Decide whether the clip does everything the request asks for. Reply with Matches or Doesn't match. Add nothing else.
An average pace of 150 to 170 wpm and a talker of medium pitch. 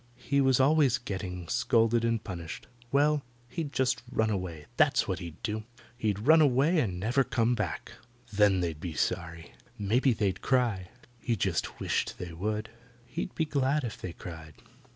Doesn't match